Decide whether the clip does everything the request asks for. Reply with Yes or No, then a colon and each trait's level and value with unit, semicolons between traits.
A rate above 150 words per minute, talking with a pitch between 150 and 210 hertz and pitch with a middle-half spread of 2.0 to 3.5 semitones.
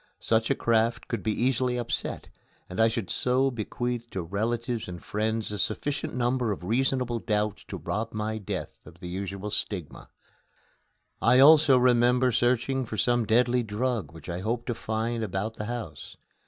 No: average, 165 wpm; low, 115 Hz; average, 2.7 semitones